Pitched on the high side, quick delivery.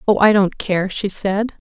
Yes: high, 200 Hz; fast, 215 wpm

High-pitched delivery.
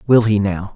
No: low, 105 Hz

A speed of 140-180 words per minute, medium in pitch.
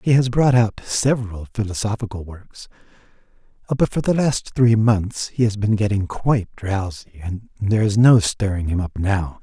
No: average, 170 wpm; low, 105 Hz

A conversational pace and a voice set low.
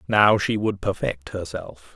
Yes: average, 155 wpm; very low, 95 Hz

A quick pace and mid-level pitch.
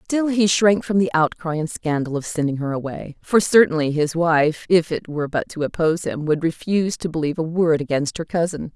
Yes: fast, 220 wpm; medium, 165 Hz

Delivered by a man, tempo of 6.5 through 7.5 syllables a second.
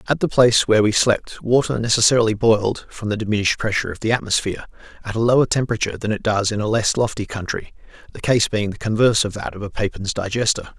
Yes: male; 6.8 syllables/s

